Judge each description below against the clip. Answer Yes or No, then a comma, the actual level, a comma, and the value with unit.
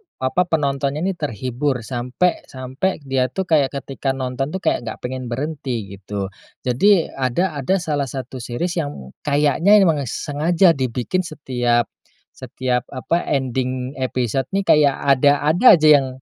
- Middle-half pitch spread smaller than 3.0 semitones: No, average, 3.7 semitones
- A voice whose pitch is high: No, low, 135 Hz